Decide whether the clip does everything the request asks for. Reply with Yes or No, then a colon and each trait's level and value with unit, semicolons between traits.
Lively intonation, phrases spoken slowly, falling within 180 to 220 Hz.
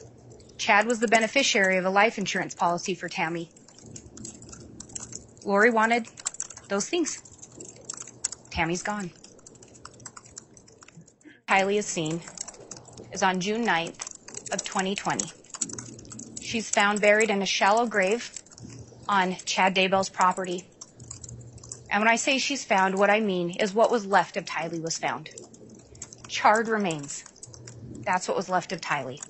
No: average, 3.8 semitones; slow, 125 wpm; high, 190 Hz